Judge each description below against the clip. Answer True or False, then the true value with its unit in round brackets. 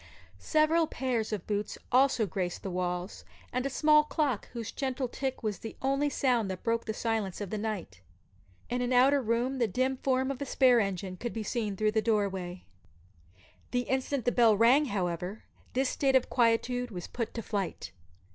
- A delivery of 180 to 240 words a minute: True (190 wpm)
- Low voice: False (230 Hz)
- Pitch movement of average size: True (4.3 semitones)